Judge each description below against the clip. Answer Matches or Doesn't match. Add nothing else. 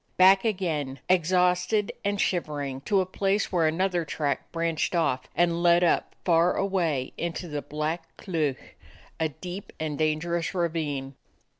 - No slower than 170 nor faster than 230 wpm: Doesn't match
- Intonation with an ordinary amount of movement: Matches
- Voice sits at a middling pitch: Matches